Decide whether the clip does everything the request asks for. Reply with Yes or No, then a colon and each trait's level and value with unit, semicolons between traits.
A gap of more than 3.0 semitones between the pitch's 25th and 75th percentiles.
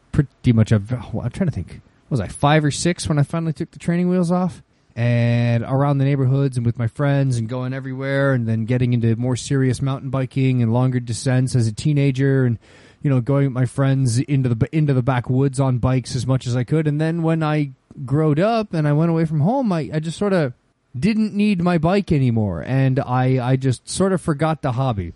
Yes: average, 3.6 semitones